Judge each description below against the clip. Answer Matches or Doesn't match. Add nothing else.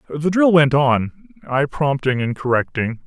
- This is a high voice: Doesn't match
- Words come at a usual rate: Matches